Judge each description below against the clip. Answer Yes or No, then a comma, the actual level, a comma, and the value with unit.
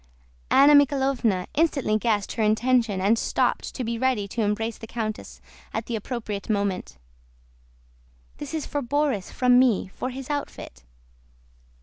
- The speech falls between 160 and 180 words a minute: No, average, 140 wpm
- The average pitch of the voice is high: Yes, high, 230 Hz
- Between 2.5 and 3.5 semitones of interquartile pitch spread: No, average, 4.0 semitones